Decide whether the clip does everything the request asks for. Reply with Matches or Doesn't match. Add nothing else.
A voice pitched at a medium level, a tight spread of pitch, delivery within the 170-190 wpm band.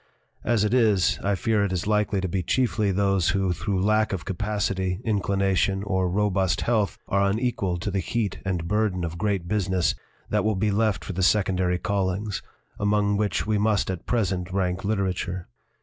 Doesn't match